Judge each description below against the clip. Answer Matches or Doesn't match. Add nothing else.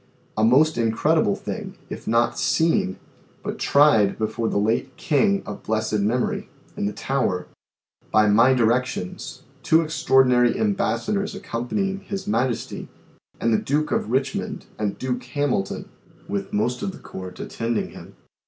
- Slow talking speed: Doesn't match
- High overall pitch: Doesn't match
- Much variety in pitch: Matches